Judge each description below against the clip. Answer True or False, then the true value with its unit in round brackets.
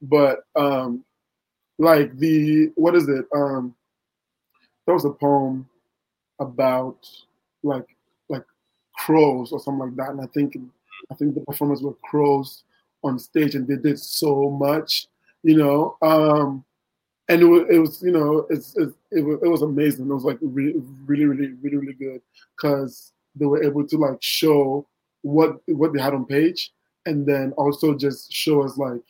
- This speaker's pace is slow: False (170 wpm)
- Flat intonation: True (2.0 semitones)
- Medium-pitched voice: True (145 Hz)